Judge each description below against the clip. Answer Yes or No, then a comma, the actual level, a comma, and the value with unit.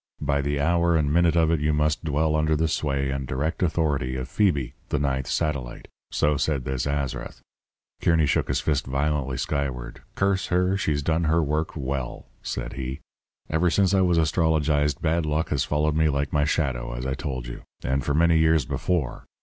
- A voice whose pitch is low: Yes, very low, 75 Hz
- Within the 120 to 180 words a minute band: No, average, 190 wpm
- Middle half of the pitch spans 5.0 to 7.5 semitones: No, average, 2.9 semitones